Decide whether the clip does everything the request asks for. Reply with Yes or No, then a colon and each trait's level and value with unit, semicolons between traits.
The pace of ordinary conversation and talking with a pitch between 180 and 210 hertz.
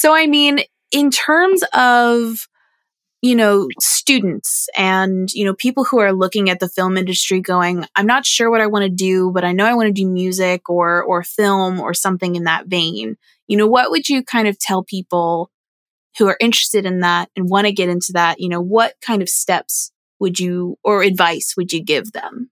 No: fast, 210 wpm; high, 190 Hz